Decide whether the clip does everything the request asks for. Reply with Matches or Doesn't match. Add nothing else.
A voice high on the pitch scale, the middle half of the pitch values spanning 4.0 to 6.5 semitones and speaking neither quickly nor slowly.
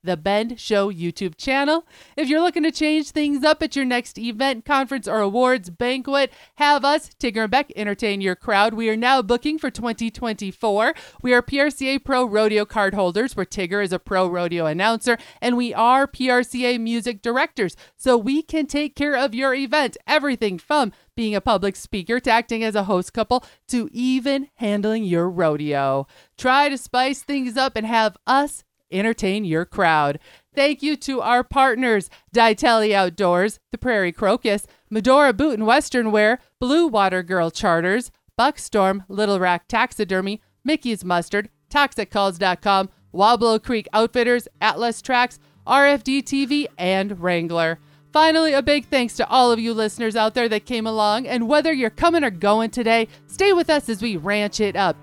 Matches